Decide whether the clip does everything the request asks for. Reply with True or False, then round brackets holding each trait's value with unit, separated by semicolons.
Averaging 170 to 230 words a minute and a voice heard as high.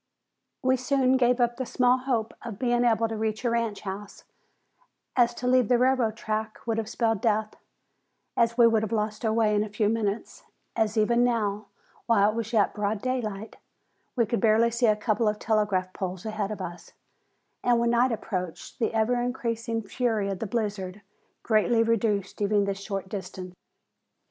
True (185 wpm; 220 Hz)